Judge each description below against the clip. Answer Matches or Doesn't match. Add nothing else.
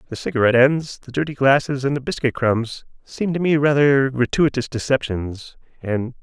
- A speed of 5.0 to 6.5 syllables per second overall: Matches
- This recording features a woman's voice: Doesn't match